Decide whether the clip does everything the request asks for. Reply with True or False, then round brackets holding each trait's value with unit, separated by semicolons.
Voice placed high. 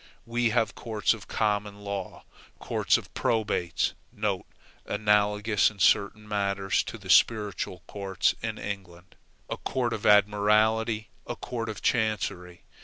False (105 Hz)